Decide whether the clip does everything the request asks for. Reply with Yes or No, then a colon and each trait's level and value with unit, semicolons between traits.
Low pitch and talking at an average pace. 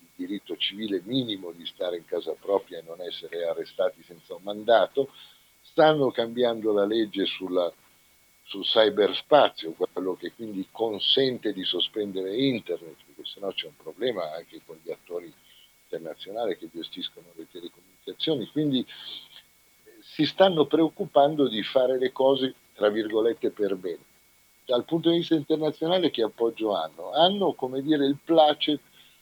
No: medium, 155 Hz; average, 140 wpm